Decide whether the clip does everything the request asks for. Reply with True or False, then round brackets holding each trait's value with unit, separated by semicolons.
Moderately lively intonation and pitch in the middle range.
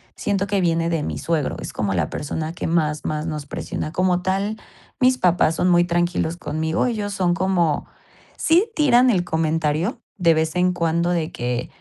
True (3.0 semitones; 170 Hz)